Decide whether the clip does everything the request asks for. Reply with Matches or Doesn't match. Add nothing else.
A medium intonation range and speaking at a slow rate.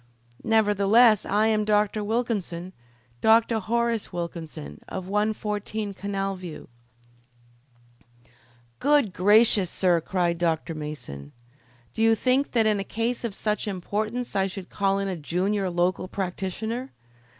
Matches